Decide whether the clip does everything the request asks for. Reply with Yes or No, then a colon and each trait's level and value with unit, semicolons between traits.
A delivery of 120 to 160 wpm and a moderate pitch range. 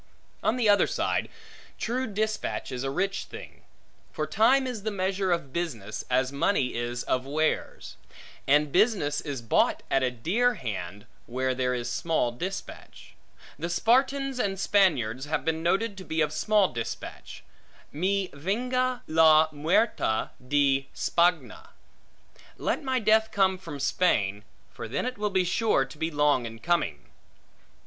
No: average, 150 wpm; wide, 7.6 semitones